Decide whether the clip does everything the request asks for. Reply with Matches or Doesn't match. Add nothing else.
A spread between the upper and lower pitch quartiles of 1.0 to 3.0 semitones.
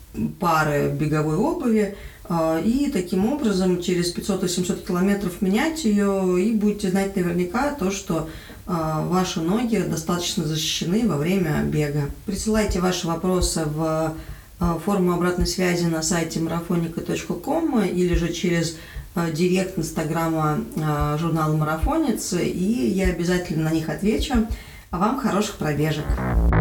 Doesn't match